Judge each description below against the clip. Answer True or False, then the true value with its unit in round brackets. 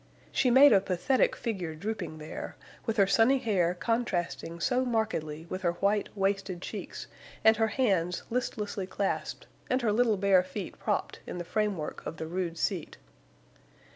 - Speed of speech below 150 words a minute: False (160 wpm)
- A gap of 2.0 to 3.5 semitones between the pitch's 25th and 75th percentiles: False (4.3 semitones)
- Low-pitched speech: False (195 Hz)